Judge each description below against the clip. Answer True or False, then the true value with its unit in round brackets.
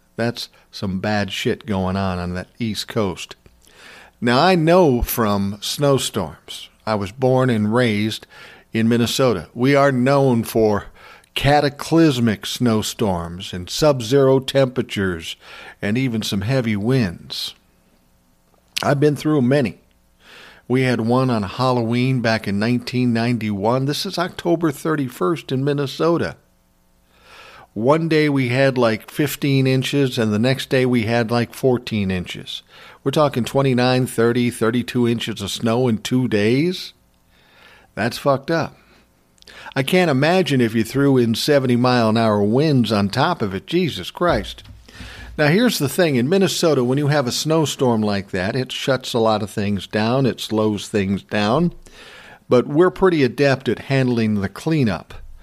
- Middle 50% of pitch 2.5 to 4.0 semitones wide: False (4.7 semitones)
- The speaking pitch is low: True (120 Hz)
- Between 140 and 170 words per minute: True (145 wpm)